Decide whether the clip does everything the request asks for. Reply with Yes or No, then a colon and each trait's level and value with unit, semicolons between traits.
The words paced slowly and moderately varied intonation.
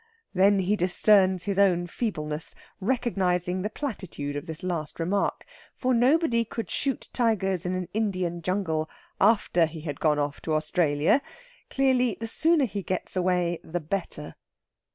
No: average, 150 wpm; average, 4.5 semitones